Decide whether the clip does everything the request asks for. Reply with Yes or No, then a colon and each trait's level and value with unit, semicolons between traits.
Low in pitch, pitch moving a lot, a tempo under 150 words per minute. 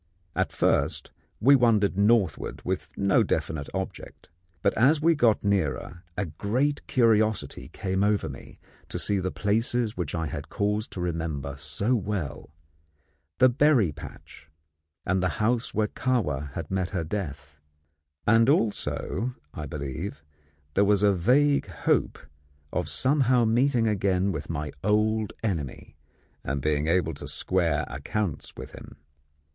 Yes: low, 100 Hz; wide, 5.8 semitones; average, 140 wpm